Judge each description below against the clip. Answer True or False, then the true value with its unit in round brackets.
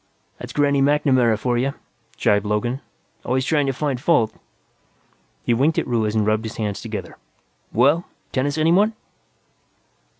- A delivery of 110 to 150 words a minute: True (140 wpm)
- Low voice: True (130 Hz)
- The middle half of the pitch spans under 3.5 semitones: False (4.5 semitones)